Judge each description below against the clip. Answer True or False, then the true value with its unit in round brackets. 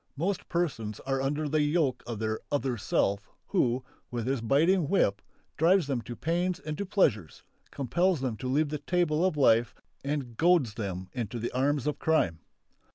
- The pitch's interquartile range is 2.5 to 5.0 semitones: False (5.6 semitones)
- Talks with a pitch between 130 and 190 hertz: True (140 Hz)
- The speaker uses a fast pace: False (175 wpm)